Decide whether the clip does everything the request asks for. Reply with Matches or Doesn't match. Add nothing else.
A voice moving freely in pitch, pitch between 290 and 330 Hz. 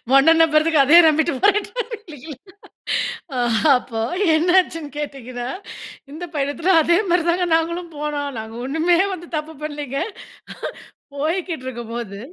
Doesn't match